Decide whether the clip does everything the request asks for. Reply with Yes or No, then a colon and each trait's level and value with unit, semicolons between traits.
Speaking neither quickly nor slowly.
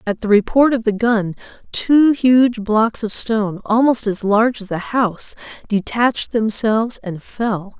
Yes: average, 160 wpm